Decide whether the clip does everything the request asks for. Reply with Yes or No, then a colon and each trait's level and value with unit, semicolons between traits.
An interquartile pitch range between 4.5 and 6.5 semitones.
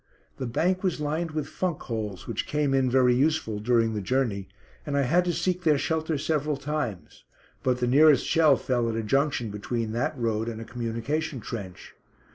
Yes: average, 5.1 semitones